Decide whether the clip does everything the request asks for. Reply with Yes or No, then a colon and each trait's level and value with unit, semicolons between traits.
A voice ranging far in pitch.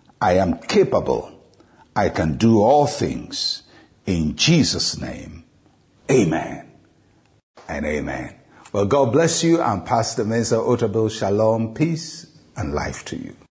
Yes: wide, 5.9 semitones